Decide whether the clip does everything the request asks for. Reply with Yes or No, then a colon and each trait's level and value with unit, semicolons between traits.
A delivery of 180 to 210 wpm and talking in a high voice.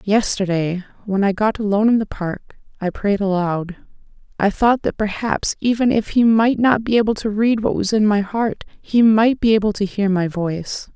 Yes: fast, 205 wpm; high, 210 Hz